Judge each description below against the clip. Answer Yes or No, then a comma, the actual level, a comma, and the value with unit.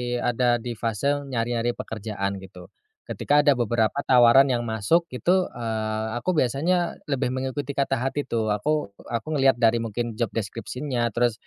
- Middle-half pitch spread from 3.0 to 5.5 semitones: Yes, average, 3.3 semitones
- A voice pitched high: No, low, 120 Hz